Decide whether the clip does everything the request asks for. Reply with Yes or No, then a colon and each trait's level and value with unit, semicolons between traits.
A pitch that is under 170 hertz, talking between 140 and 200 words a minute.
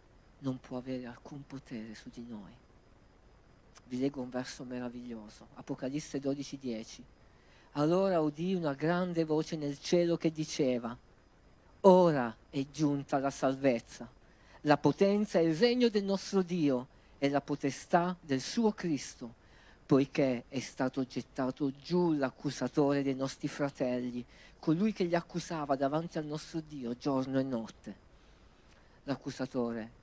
No: medium, 140 Hz; average, 130 wpm